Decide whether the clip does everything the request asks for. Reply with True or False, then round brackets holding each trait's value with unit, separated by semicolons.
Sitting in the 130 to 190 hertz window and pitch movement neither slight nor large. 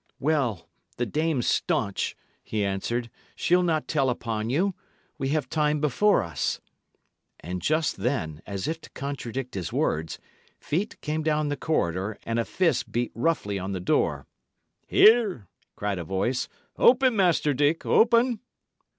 False (135 Hz; 7.6 semitones)